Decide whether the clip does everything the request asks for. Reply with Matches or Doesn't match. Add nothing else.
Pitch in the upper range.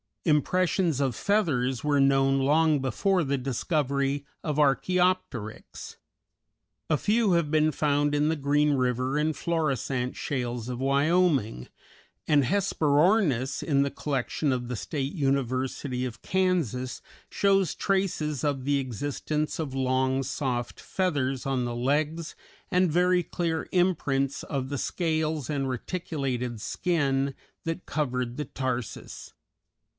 Doesn't match